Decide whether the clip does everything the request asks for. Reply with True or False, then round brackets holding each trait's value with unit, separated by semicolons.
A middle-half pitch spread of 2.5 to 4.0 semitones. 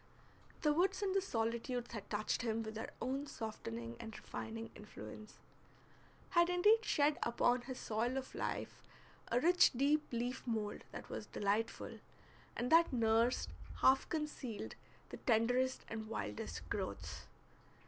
False (4.7 semitones)